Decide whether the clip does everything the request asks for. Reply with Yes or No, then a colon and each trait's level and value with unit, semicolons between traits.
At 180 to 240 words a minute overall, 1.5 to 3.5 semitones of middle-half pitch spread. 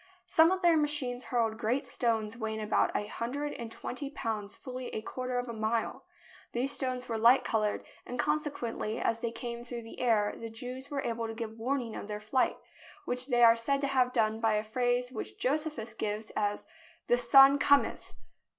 Yes: average, 195 wpm; average, 2.7 semitones